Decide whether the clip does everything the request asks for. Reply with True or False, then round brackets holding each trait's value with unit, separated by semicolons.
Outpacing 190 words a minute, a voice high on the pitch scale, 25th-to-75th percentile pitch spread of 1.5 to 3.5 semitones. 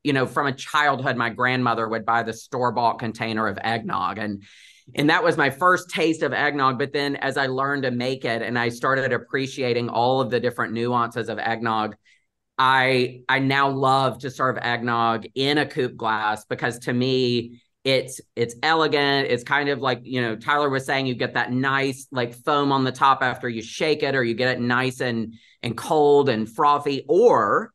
False (200 wpm; 125 Hz; 2.7 semitones)